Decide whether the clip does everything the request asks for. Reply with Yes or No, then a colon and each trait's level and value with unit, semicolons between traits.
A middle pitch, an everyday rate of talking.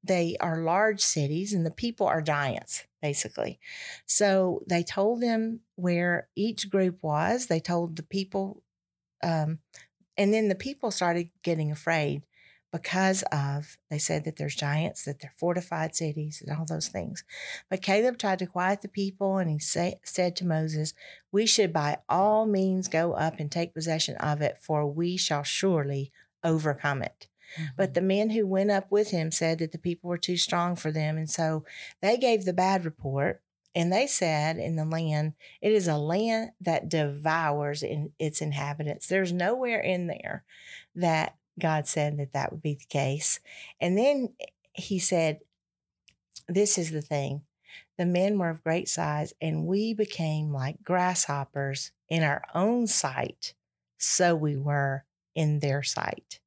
Yes: medium, 170 Hz; average, 165 wpm